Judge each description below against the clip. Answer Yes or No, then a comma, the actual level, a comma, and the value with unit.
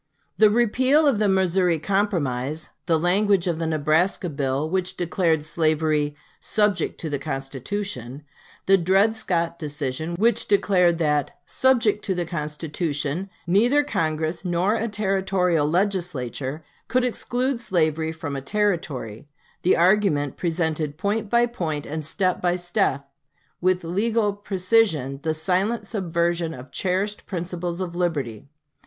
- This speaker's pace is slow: Yes, slow, 130 wpm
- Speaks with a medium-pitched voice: Yes, medium, 175 Hz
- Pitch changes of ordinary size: Yes, average, 4.5 semitones